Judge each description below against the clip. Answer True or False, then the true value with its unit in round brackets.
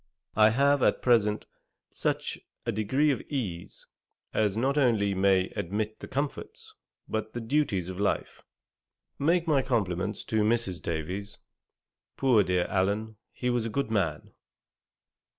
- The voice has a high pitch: False (110 Hz)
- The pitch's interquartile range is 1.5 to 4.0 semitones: False (4.5 semitones)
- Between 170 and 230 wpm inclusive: False (135 wpm)